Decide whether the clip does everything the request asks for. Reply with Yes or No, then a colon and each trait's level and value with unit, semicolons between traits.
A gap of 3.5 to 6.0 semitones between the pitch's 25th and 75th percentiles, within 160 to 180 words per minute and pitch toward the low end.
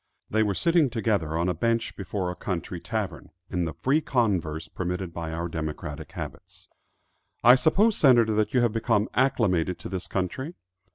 Yes: wide, 5.6 semitones; average, 170 wpm; low, 100 Hz